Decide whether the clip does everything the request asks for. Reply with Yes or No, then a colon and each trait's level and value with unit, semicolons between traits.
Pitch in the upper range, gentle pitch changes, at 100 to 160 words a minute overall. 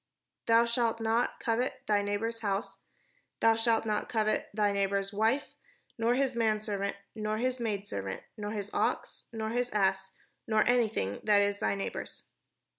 Yes: high, 215 Hz; narrow, 2.2 semitones; average, 155 wpm